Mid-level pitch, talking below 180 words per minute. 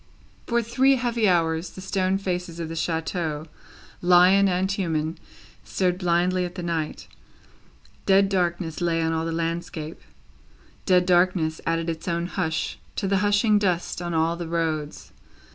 Yes: medium, 175 Hz; average, 150 wpm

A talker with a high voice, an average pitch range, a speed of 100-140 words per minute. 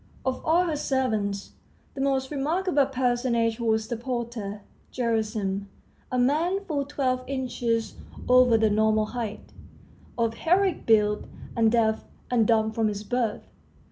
Yes: high, 235 Hz; average, 3.4 semitones; slow, 135 wpm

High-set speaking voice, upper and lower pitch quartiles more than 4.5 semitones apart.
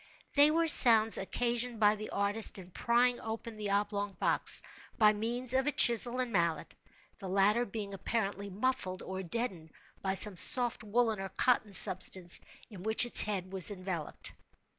No: high, 210 Hz; average, 3.7 semitones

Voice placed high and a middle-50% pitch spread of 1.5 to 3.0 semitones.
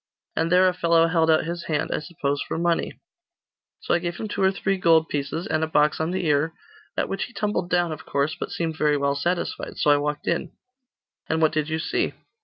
No: medium, 160 Hz; narrow, 2.4 semitones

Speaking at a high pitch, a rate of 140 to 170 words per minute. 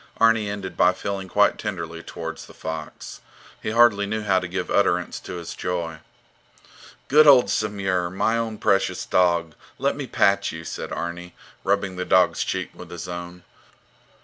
No: very low, 95 Hz; average, 165 wpm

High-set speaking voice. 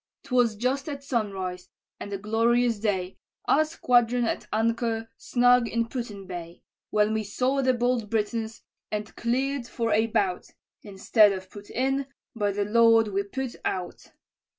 Yes: high, 225 Hz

